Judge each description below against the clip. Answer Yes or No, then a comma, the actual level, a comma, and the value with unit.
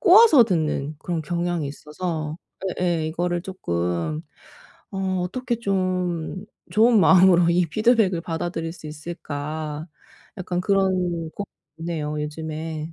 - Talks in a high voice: No, medium, 170 Hz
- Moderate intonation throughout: Yes, average, 3.0 semitones